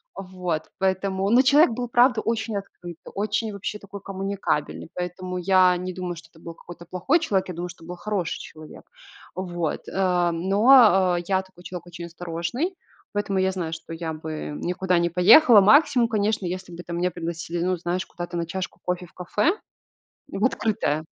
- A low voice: No, medium, 185 Hz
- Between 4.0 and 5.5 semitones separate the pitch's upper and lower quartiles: No, average, 2.7 semitones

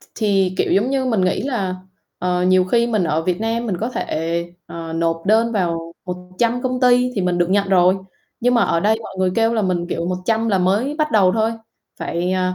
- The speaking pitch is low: No, high, 190 Hz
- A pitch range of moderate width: Yes, average, 4.1 semitones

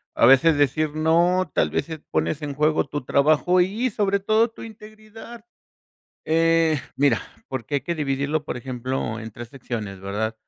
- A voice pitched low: No, medium, 155 Hz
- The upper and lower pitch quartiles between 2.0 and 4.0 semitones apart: No, wide, 5.4 semitones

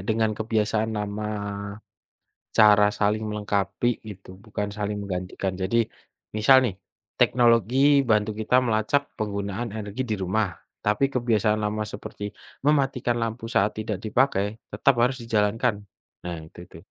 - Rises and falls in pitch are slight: Yes, narrow, 2.1 semitones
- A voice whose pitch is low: Yes, low, 110 Hz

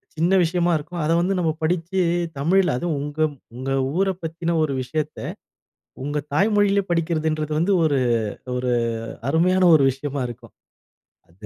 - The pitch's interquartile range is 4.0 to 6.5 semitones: No, average, 3.3 semitones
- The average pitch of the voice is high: No, medium, 160 Hz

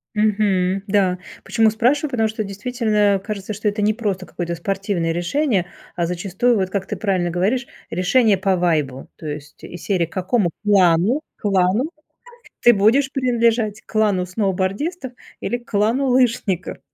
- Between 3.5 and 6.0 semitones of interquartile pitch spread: Yes, average, 3.9 semitones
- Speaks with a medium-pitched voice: No, high, 205 Hz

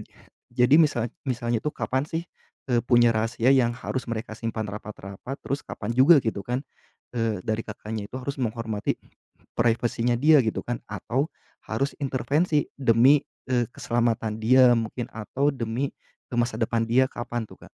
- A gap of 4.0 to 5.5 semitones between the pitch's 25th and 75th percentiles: No, average, 2.7 semitones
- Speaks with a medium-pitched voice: No, low, 120 Hz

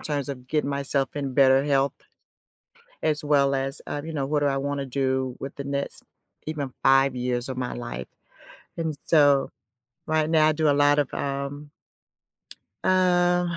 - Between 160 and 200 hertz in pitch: No, medium, 140 Hz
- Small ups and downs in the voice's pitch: Yes, narrow, 2.0 semitones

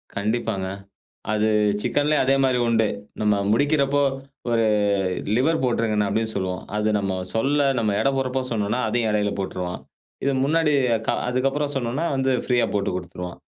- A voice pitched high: No, low, 115 Hz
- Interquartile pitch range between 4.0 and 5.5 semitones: Yes, average, 4.5 semitones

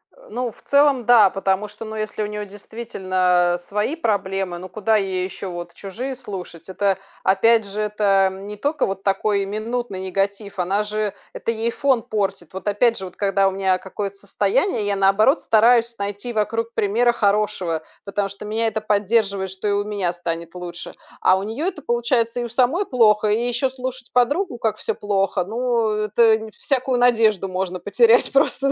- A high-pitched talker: Yes, high, 210 Hz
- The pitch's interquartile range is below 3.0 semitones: No, average, 3.3 semitones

